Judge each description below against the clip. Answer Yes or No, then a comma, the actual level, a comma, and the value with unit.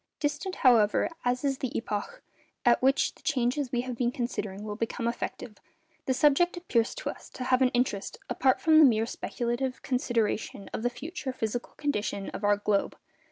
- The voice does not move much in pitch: No, average, 3.3 semitones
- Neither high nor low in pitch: No, high, 245 Hz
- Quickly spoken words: No, average, 180 wpm